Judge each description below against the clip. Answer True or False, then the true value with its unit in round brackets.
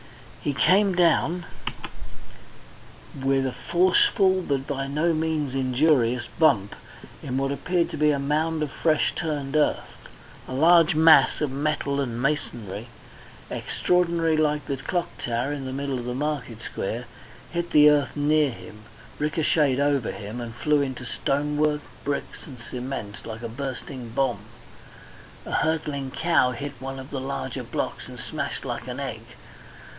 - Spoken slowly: False (150 wpm)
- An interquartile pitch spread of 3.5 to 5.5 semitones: False (3.1 semitones)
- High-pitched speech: False (140 Hz)